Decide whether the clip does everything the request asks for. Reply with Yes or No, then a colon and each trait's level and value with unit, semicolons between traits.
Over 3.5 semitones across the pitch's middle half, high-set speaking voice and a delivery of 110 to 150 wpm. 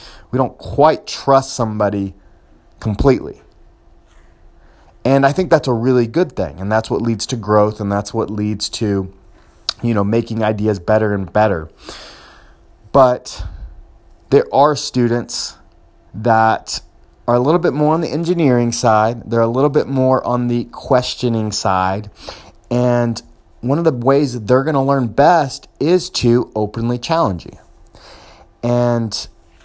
No: average, 4.2 semitones; low, 115 Hz; average, 145 wpm